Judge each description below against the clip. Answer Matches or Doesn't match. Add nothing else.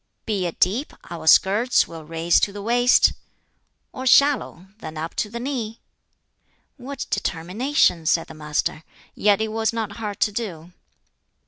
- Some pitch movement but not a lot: Doesn't match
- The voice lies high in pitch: Matches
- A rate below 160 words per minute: Matches